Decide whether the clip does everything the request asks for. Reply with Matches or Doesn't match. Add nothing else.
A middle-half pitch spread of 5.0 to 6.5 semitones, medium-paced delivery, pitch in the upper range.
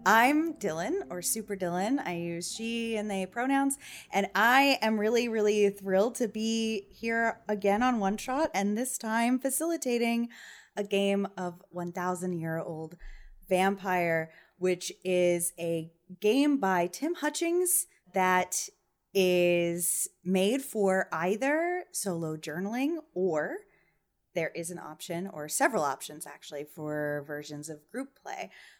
Doesn't match